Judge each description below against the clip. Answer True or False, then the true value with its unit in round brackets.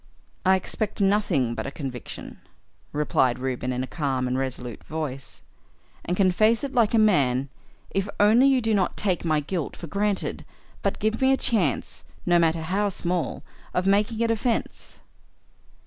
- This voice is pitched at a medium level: True (180 Hz)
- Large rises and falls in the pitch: True (7.3 semitones)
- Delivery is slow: False (165 wpm)